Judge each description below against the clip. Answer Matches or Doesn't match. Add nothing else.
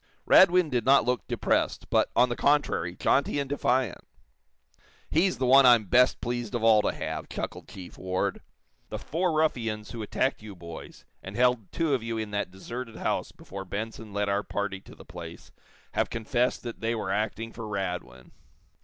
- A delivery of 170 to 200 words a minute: Matches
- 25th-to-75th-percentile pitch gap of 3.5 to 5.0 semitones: Matches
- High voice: Doesn't match